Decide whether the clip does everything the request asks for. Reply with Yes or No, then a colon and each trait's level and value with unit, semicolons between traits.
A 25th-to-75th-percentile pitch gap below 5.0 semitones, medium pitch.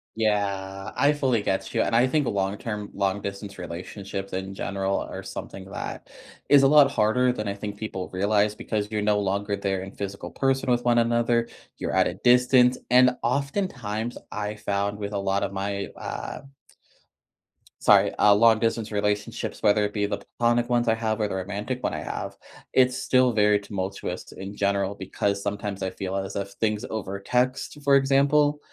No: average, 3.3 semitones; low, 105 Hz